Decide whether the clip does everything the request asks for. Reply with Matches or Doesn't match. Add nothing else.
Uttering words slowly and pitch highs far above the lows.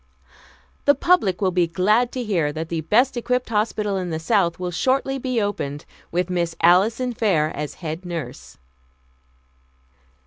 Doesn't match